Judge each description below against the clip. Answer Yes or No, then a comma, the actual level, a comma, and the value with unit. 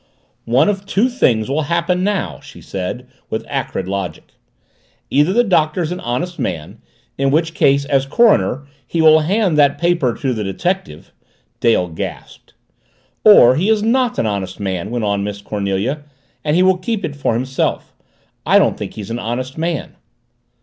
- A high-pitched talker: No, medium, 140 Hz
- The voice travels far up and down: Yes, wide, 8.4 semitones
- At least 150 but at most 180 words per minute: Yes, average, 170 wpm